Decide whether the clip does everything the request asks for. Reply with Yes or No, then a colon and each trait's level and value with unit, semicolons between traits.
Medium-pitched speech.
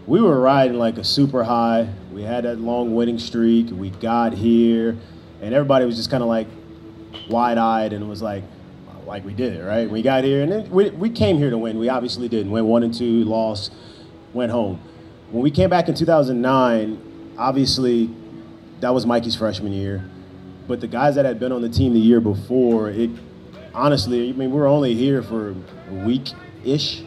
No: low, 115 Hz